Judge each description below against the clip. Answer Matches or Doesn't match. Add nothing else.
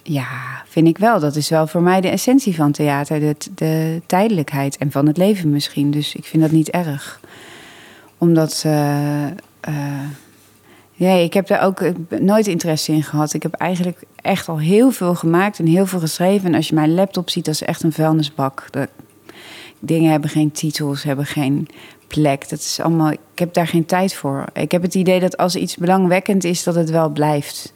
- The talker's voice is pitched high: Doesn't match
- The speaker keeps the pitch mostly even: Doesn't match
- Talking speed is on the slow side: Doesn't match